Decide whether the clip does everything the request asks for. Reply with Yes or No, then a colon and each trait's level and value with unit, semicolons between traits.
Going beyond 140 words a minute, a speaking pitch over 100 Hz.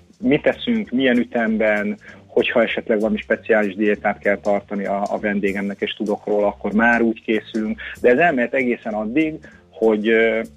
Yes: fast, 155 wpm; low, 110 Hz